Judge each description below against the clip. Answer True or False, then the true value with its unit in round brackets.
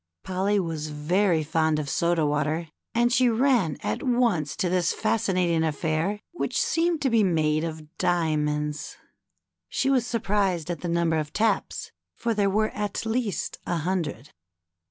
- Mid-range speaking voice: True (175 Hz)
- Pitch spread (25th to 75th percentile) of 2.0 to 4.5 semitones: False (5.2 semitones)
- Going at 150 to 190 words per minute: True (155 wpm)